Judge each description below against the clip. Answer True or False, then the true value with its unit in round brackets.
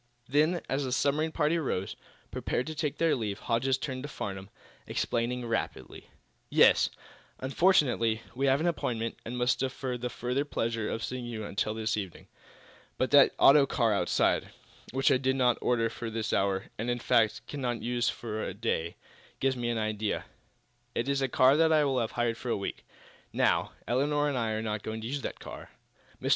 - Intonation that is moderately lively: True (3.5 semitones)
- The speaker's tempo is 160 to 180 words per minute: False (190 wpm)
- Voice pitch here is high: False (125 Hz)